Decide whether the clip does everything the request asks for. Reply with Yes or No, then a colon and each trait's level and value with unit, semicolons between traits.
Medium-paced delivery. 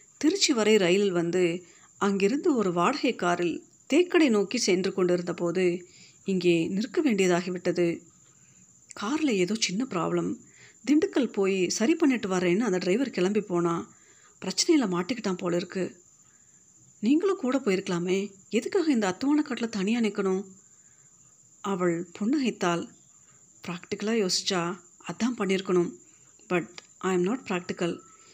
Yes: average, 110 wpm